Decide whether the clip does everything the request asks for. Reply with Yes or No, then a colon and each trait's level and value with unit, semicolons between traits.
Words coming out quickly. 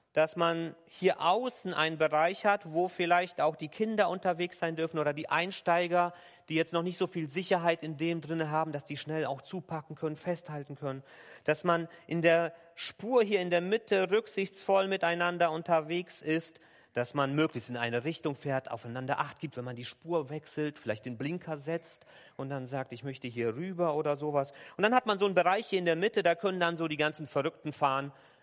Yes: fast, 205 wpm